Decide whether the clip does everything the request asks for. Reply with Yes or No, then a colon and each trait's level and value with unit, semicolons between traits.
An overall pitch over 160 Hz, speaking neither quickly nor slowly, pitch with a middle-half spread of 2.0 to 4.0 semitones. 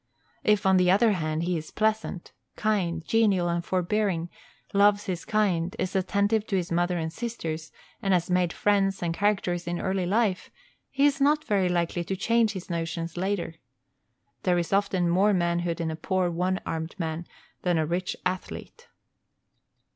Yes: medium, 185 Hz; average, 170 wpm; average, 3.0 semitones